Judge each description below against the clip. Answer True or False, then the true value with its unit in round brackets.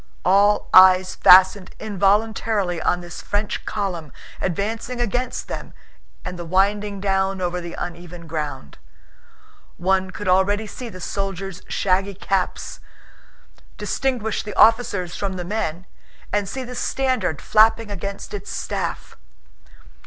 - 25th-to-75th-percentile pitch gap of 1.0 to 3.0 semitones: True (2.5 semitones)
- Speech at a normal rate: False (120 wpm)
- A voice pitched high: True (195 Hz)